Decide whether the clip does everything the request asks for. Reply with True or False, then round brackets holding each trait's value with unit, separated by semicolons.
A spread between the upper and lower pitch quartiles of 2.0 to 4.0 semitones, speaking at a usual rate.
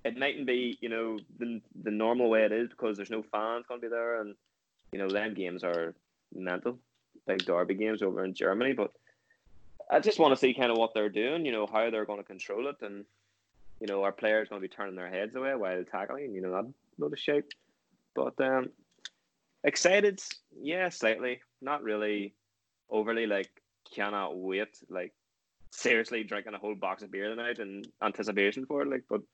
True (3.3 semitones; 190 wpm)